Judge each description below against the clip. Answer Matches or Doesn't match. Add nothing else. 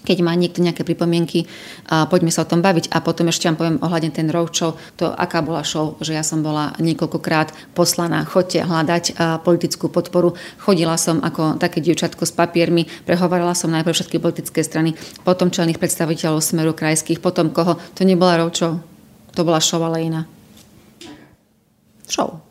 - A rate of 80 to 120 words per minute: Doesn't match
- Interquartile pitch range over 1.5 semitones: Doesn't match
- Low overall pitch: Doesn't match